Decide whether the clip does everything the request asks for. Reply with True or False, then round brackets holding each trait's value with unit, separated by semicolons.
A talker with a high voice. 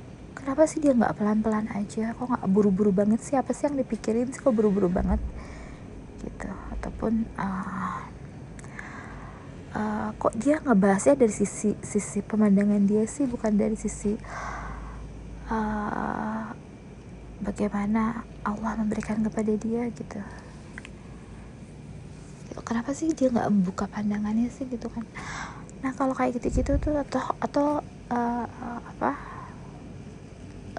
True (220 Hz)